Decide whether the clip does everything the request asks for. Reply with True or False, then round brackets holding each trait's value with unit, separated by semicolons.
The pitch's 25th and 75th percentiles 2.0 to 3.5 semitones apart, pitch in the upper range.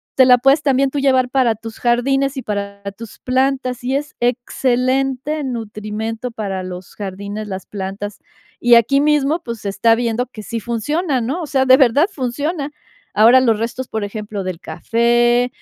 False (3.9 semitones; 240 Hz)